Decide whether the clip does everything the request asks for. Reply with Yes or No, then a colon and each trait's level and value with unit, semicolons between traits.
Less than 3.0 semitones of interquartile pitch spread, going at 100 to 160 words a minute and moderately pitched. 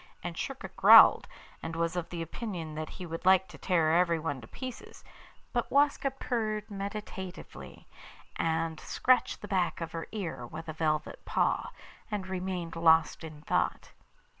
No: average, 3.6 semitones; average, 150 wpm; medium, 170 Hz